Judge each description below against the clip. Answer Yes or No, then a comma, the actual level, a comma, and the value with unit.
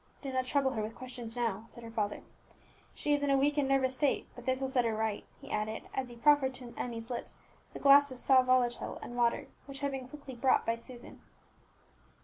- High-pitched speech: Yes, very high, 255 Hz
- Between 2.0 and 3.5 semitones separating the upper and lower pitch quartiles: Yes, narrow, 2.5 semitones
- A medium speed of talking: No, fast, 225 wpm